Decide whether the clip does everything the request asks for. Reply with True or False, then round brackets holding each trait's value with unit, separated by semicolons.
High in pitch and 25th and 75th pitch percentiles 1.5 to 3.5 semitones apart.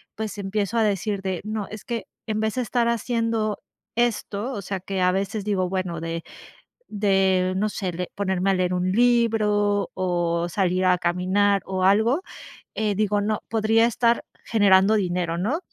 True (200 Hz; 2.8 semitones)